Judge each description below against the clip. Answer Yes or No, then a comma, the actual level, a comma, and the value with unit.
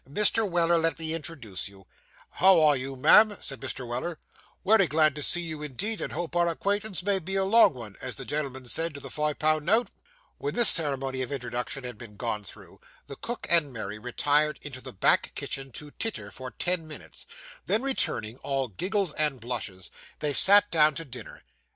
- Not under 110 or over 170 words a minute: No, average, 195 wpm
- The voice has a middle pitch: Yes, medium, 150 Hz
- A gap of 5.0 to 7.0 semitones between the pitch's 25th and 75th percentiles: Yes, average, 5.3 semitones